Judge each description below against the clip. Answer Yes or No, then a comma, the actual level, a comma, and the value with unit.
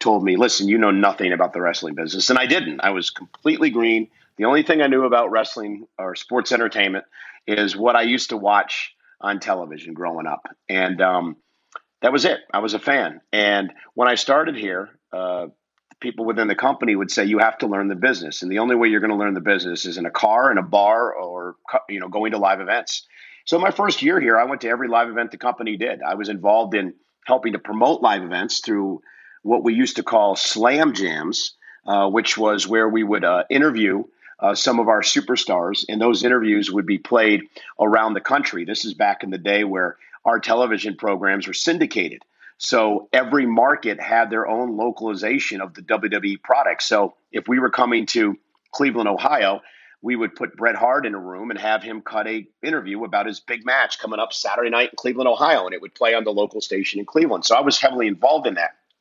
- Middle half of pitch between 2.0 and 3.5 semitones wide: Yes, average, 2.8 semitones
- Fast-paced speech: Yes, fast, 220 wpm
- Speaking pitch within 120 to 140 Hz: No, low, 110 Hz